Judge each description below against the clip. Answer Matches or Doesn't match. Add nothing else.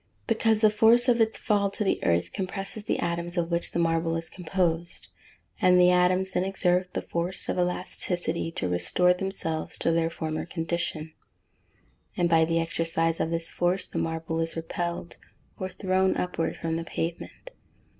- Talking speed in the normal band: Matches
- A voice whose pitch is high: Doesn't match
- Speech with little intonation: Matches